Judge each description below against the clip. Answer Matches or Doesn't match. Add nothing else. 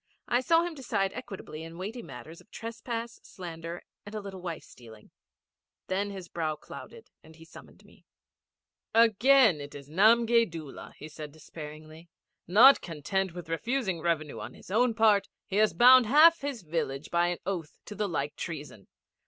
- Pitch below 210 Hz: Matches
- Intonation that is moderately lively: Doesn't match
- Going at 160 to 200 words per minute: Matches